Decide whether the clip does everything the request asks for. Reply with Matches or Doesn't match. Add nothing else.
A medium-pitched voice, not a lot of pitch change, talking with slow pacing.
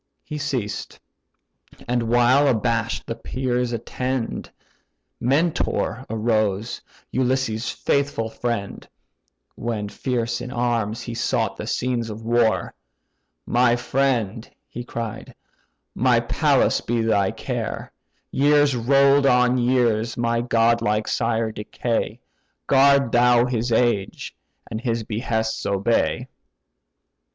Doesn't match